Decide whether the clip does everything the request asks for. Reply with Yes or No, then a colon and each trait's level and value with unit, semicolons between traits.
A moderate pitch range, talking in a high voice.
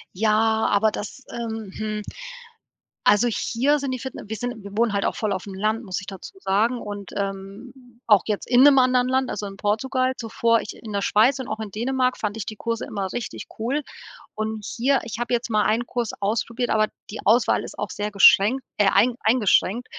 Yes: average, 3.0 semitones; high, 220 Hz